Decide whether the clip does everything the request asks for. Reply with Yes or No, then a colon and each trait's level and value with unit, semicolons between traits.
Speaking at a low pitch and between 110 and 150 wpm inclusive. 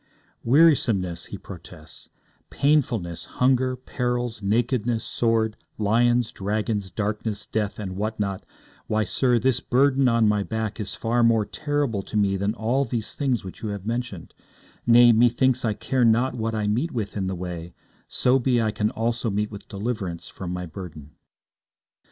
No: low, 110 Hz; average, 160 wpm